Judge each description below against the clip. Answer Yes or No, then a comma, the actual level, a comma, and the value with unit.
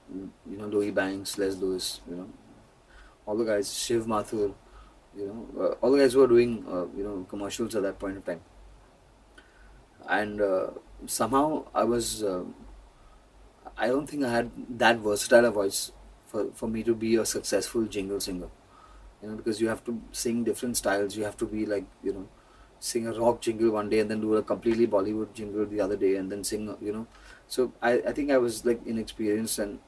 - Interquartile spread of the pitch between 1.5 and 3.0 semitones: Yes, narrow, 2.5 semitones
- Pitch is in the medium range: No, low, 110 Hz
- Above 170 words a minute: Yes, average, 200 wpm